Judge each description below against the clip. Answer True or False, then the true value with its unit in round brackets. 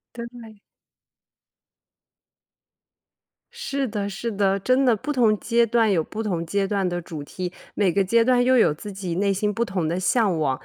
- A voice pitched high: True (205 Hz)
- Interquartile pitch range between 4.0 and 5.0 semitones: True (4.3 semitones)